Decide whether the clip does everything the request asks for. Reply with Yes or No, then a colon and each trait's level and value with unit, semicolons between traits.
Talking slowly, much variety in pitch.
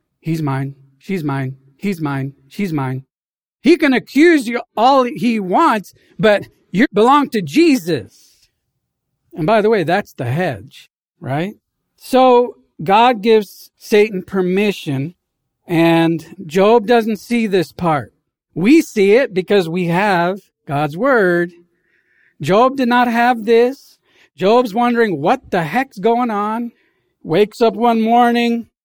Yes: slow, 130 wpm; wide, 6.2 semitones